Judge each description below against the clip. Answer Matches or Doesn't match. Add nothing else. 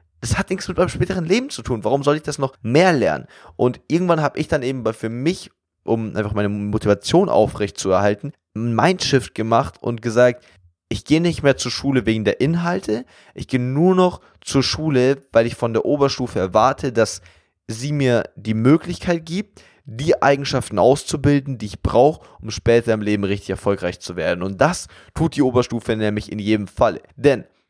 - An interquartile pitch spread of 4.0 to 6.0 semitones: Matches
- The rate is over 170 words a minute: Matches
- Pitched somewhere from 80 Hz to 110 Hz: Doesn't match